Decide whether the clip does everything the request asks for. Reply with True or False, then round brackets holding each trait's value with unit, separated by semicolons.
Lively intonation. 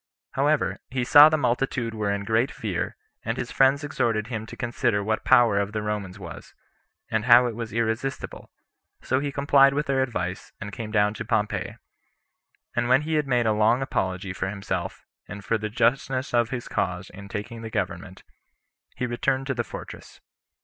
False (4.1 semitones)